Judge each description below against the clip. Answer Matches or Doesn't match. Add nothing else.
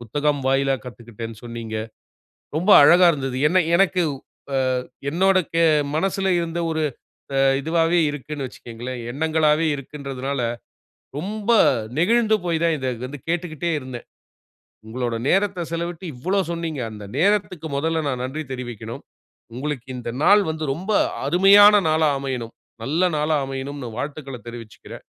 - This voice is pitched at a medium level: Matches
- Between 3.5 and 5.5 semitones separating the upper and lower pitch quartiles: Matches